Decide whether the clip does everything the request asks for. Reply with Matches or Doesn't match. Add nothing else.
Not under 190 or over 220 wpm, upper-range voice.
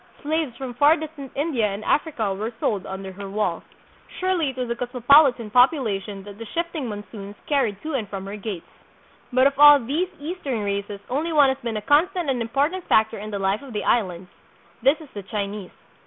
Matches